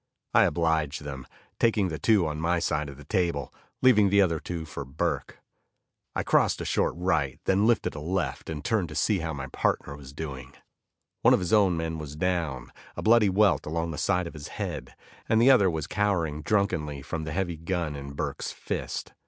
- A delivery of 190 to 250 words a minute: Yes, average, 200 wpm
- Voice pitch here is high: No, very low, 80 Hz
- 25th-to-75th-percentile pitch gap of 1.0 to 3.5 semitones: No, average, 4.4 semitones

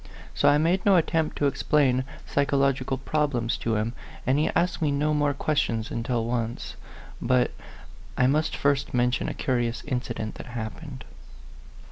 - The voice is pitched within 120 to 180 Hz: Yes, low, 135 Hz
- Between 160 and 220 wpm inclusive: No, average, 150 wpm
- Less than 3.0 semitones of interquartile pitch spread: No, average, 3.6 semitones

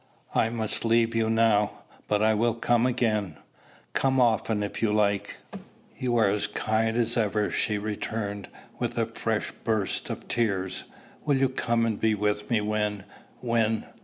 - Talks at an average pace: Yes, average, 160 wpm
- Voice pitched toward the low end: Yes, low, 110 Hz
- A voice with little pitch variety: Yes, narrow, 1.9 semitones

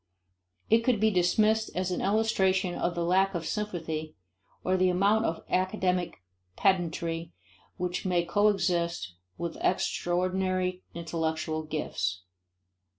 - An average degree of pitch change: No, narrow, 2.3 semitones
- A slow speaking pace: Yes, slow, 115 wpm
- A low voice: No, medium, 180 Hz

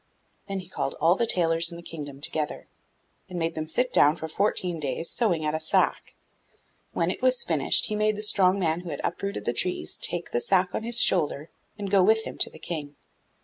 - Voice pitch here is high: No, medium, 175 Hz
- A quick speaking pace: Yes, fast, 220 wpm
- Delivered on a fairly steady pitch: No, average, 4.0 semitones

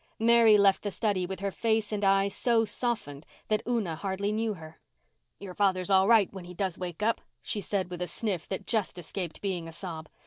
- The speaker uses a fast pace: Yes, fast, 210 wpm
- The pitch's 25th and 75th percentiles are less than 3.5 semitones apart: Yes, average, 3.1 semitones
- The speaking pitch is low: No, high, 195 Hz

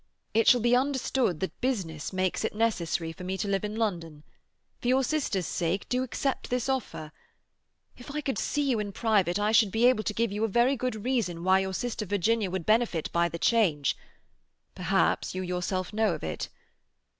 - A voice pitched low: No, high, 210 Hz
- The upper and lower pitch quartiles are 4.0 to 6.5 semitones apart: Yes, average, 4.9 semitones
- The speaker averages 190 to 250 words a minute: Yes, average, 195 wpm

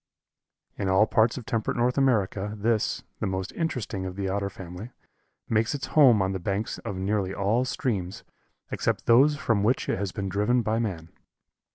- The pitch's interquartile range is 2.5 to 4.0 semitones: Yes, average, 3.7 semitones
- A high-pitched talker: No, low, 105 Hz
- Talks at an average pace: Yes, average, 180 wpm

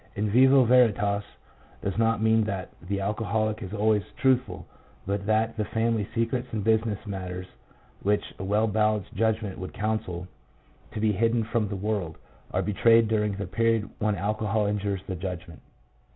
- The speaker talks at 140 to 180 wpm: Yes, average, 160 wpm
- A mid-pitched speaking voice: No, low, 105 Hz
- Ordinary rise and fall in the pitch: No, narrow, 2.0 semitones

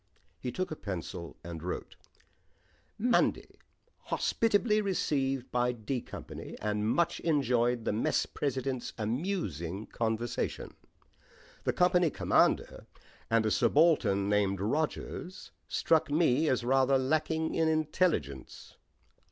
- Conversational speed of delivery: No, slow, 110 wpm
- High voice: No, low, 130 Hz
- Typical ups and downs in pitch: No, wide, 6.8 semitones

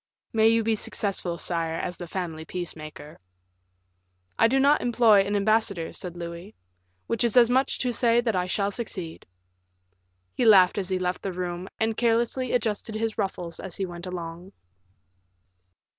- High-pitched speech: Yes, high, 195 Hz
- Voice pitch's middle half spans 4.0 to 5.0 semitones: Yes, average, 4.4 semitones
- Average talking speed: Yes, average, 165 wpm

